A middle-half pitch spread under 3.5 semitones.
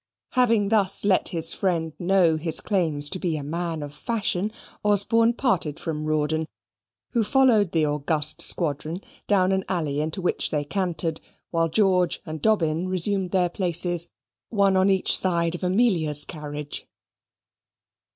No: average, 3.8 semitones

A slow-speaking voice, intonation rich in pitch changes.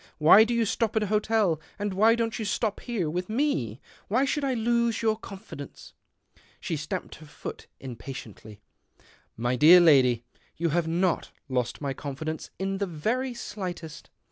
No: average, 170 wpm; wide, 6.9 semitones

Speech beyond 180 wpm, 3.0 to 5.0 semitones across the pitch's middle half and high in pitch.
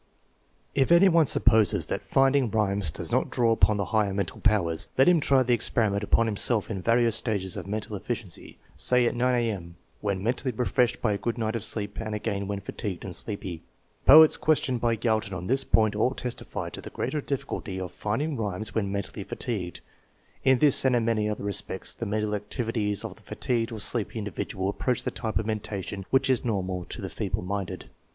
No: average, 200 wpm; average, 3.4 semitones; low, 110 Hz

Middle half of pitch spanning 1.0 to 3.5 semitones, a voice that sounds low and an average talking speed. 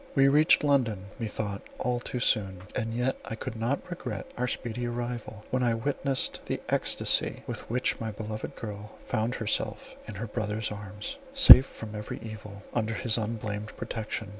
Yes: narrow, 2.6 semitones; low, 115 Hz; average, 165 wpm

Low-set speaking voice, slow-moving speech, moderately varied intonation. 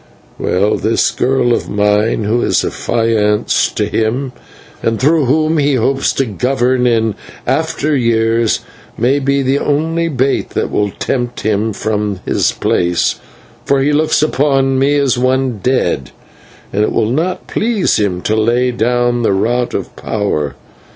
No: low, 120 Hz; average, 150 wpm; average, 3.9 semitones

